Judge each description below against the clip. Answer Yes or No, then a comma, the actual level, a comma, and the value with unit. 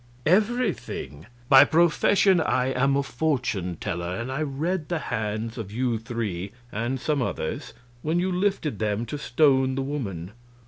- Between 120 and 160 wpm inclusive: Yes, average, 150 wpm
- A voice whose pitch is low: Yes, low, 130 Hz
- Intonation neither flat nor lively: No, wide, 6.4 semitones